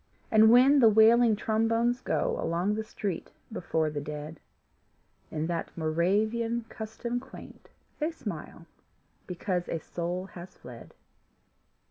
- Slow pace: Yes, slow, 120 wpm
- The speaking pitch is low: No, high, 210 Hz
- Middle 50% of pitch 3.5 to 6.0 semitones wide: Yes, wide, 5.5 semitones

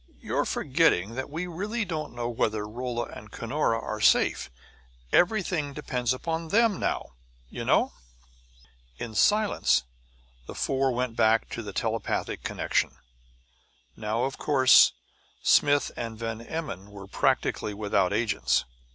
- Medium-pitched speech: No, low, 120 Hz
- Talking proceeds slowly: Yes, slow, 125 wpm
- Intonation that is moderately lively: No, wide, 5.7 semitones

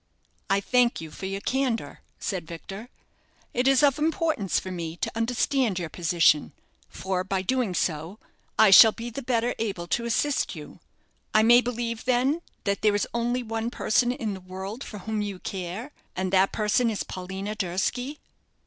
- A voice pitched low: No, high, 220 Hz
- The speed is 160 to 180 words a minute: Yes, average, 175 wpm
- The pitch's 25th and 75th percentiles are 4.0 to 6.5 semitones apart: Yes, average, 4.3 semitones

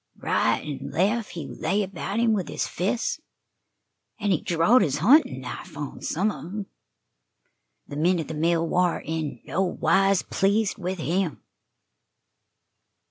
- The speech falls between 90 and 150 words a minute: Yes, average, 145 wpm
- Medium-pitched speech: Yes, medium, 180 Hz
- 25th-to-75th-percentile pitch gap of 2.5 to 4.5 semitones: Yes, average, 4.1 semitones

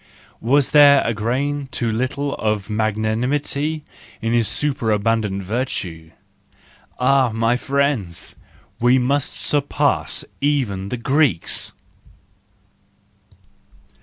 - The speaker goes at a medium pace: No, slow, 90 wpm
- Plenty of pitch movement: No, average, 4.4 semitones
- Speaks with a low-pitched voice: Yes, low, 125 Hz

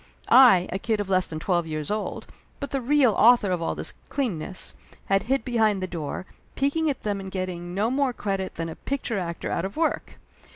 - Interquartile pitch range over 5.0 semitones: Yes, wide, 5.5 semitones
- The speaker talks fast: Yes, fast, 210 wpm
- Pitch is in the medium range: No, high, 200 Hz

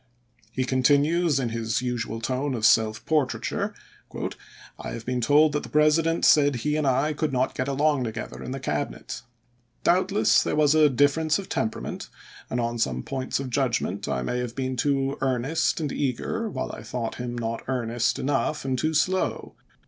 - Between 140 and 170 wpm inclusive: No, average, 185 wpm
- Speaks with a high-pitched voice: No, low, 135 Hz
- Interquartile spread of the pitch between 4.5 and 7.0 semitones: No, average, 3.8 semitones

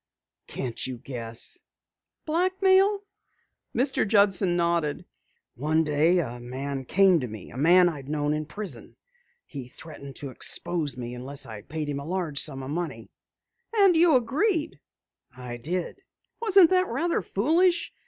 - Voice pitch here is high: No, medium, 160 Hz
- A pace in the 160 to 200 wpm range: No, average, 145 wpm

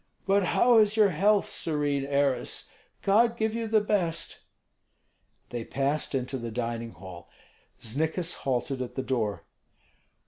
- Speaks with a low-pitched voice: No, medium, 145 Hz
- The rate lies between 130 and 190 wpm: Yes, slow, 135 wpm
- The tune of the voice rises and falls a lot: Yes, wide, 8.6 semitones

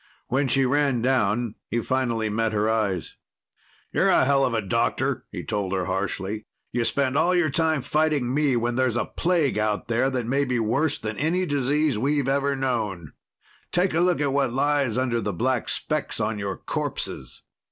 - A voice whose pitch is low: Yes, low, 130 Hz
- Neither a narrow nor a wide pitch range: Yes, average, 4.4 semitones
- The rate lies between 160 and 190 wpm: Yes, average, 180 wpm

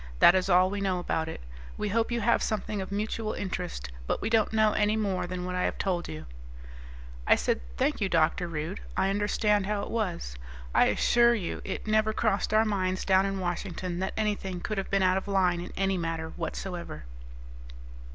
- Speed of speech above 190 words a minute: Yes, average, 200 wpm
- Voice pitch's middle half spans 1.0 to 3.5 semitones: Yes, average, 3.0 semitones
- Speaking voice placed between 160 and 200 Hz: Yes, high, 190 Hz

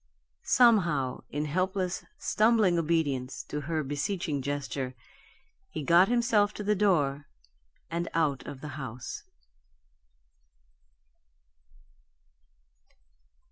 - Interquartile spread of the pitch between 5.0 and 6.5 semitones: Yes, wide, 5.6 semitones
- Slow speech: Yes, slow, 90 wpm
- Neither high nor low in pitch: Yes, medium, 160 Hz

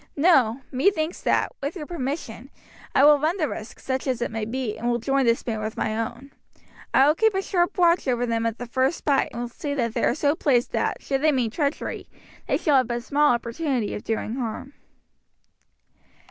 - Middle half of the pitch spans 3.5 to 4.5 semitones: Yes, average, 4.1 semitones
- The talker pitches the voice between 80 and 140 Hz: No, very high, 265 Hz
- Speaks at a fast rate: Yes, fast, 215 wpm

